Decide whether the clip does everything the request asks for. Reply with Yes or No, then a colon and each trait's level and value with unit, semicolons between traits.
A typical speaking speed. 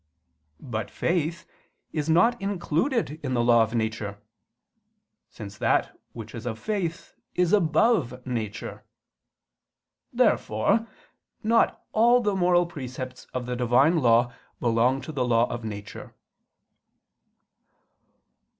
No: slow, 115 wpm